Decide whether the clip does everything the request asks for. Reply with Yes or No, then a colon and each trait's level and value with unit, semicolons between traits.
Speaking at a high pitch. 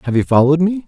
No: medium, 155 Hz